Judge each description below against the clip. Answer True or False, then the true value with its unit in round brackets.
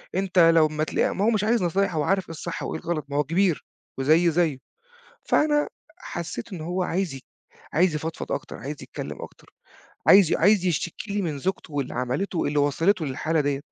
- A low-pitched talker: False (165 Hz)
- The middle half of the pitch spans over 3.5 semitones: True (4.1 semitones)